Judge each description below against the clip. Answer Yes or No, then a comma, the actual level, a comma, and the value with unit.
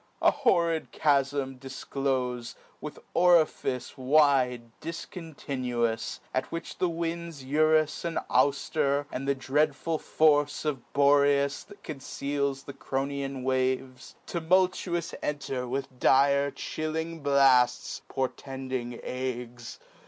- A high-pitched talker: No, medium, 140 Hz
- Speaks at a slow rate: Yes, slow, 105 wpm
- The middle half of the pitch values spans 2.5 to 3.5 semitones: Yes, average, 3.1 semitones